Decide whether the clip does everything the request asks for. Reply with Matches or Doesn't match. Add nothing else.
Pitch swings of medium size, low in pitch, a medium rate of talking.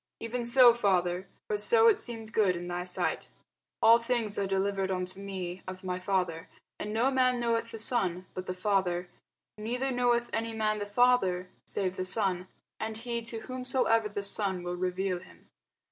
Doesn't match